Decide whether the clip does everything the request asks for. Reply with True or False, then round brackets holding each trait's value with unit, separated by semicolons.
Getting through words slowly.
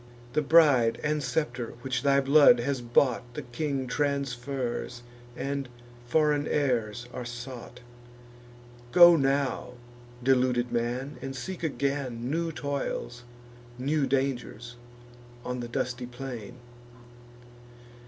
True (105 wpm)